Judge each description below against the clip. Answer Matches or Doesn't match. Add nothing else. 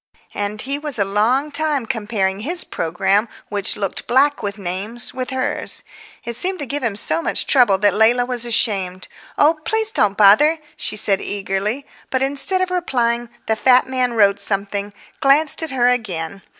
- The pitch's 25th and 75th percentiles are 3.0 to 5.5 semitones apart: Matches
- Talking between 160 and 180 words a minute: Matches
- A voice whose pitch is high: Matches